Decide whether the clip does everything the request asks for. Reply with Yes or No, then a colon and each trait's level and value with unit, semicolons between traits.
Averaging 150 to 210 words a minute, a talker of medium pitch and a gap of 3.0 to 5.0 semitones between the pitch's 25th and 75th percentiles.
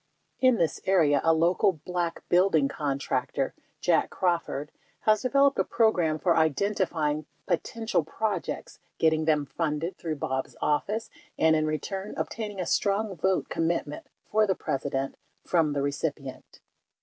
No: slow, 135 wpm; medium, 165 Hz; average, 4.6 semitones